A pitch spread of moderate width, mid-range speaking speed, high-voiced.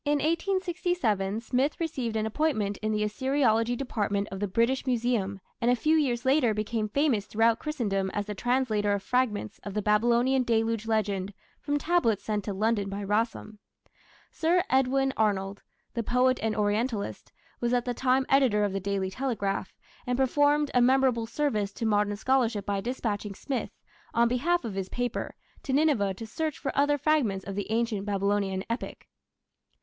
Yes: average, 4.3 semitones; average, 170 wpm; high, 230 Hz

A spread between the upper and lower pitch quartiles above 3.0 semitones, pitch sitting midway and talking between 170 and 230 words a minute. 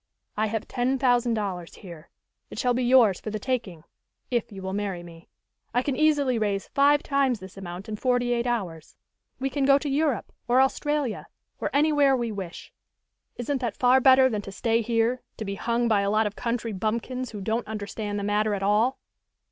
No: average, 4.1 semitones; high, 230 Hz; average, 200 wpm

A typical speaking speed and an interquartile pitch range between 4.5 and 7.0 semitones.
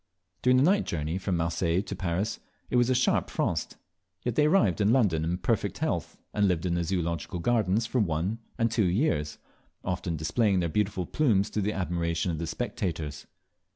Yes: average, 190 wpm; average, 5.2 semitones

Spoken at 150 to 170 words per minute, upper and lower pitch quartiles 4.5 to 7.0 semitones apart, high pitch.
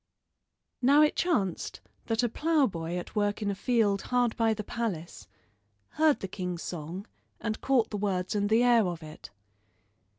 Yes: average, 165 wpm; average, 4.9 semitones; high, 210 Hz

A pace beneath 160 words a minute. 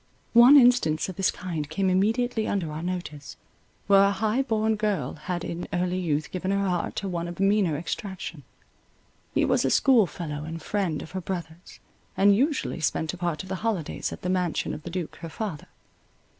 No: average, 190 wpm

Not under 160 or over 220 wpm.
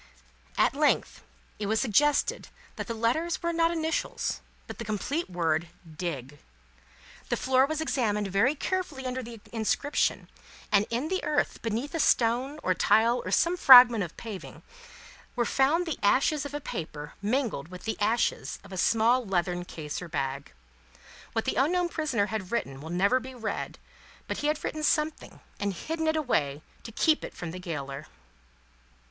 Yes: average, 170 wpm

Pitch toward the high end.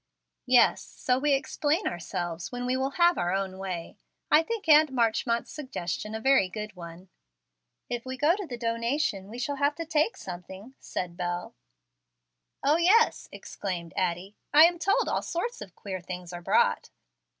Yes: high, 235 Hz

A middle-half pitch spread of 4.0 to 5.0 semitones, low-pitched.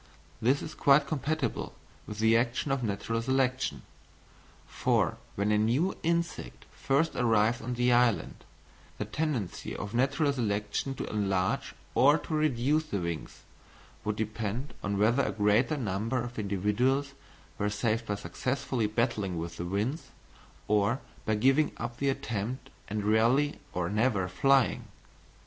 Yes: average, 4.5 semitones; low, 115 Hz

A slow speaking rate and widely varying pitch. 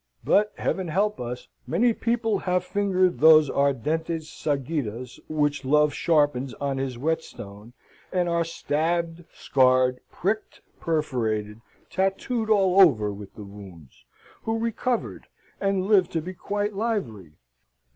Yes: slow, 125 wpm; wide, 7.1 semitones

